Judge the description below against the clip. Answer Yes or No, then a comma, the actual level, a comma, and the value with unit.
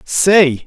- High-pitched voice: No, medium, 165 Hz